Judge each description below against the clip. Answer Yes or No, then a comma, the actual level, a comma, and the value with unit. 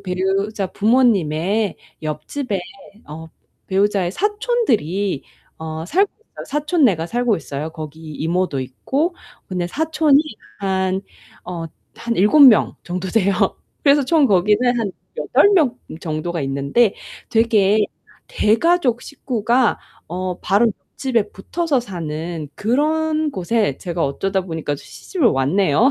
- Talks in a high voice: Yes, high, 200 Hz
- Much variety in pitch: Yes, wide, 6.8 semitones